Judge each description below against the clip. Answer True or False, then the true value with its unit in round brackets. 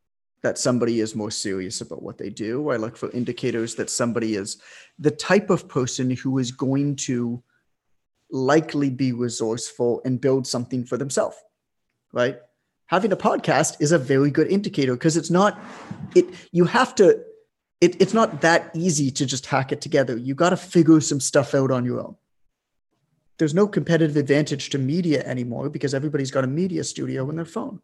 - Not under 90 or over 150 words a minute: False (180 wpm)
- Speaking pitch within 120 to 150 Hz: True (140 Hz)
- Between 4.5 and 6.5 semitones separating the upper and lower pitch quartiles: True (5.1 semitones)